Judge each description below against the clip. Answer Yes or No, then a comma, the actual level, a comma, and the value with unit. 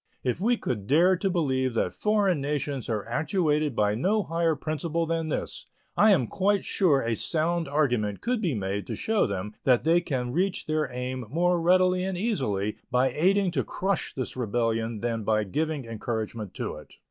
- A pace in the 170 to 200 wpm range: Yes, average, 180 wpm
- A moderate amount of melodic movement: No, wide, 7.1 semitones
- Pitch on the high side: No, medium, 150 Hz